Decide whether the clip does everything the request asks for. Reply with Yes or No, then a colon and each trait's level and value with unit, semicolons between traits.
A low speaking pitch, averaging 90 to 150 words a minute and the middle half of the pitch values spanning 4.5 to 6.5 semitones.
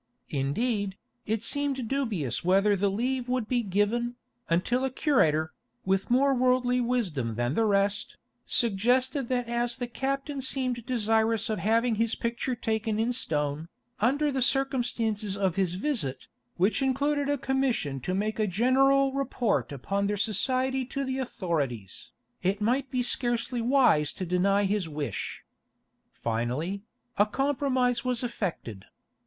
No: high, 230 Hz; average, 140 wpm; average, 4.9 semitones